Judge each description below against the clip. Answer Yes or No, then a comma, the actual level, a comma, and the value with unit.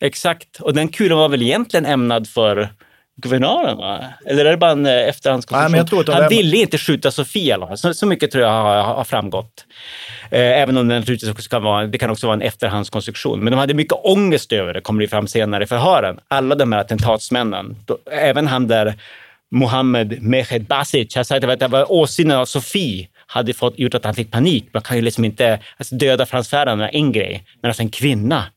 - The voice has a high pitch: No, low, 125 Hz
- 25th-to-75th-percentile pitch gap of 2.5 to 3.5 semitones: No, average, 4.1 semitones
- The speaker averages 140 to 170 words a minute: No, average, 190 wpm